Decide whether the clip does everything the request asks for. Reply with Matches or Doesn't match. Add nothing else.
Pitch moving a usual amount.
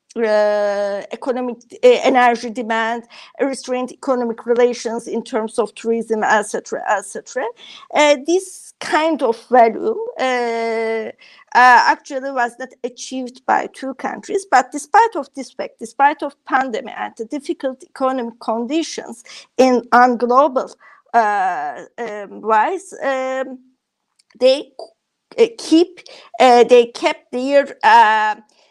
Matches